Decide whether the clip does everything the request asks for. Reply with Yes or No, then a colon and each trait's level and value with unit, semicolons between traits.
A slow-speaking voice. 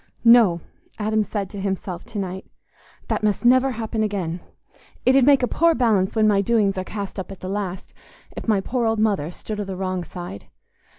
No: average, 200 wpm